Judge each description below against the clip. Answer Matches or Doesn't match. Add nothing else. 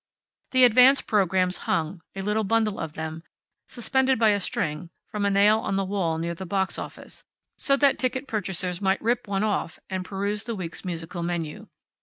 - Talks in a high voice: Matches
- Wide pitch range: Doesn't match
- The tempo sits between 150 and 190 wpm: Matches